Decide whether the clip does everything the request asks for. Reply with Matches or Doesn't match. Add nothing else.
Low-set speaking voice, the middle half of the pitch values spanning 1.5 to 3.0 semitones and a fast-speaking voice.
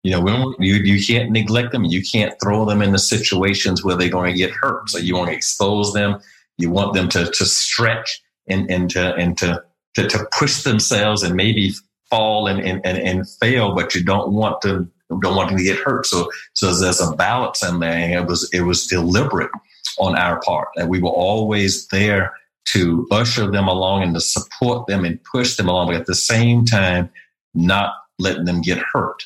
Matches